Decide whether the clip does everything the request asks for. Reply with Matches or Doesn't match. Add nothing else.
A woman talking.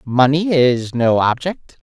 Matches